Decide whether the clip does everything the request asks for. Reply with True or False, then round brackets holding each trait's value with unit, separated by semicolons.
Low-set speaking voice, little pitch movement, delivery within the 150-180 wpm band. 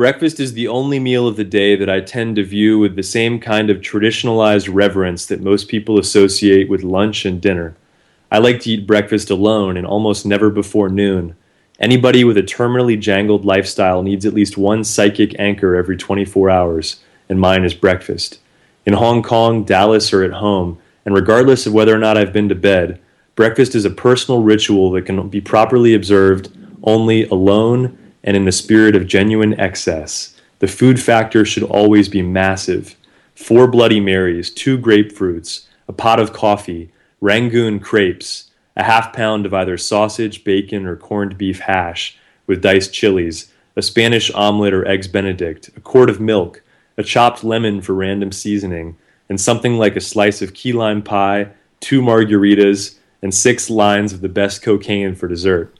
True (105 Hz; 2.3 semitones; 175 wpm)